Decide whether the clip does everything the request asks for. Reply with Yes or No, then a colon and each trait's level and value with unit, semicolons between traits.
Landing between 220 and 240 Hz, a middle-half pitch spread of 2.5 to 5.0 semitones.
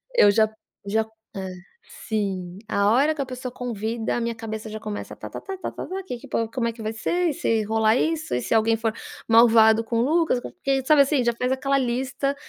Yes: high, 230 Hz; average, 3.6 semitones